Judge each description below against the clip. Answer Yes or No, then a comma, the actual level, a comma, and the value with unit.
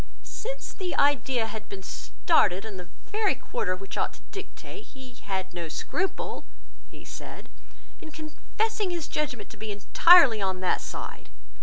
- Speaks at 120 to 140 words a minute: No, average, 155 wpm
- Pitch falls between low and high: No, very high, 255 Hz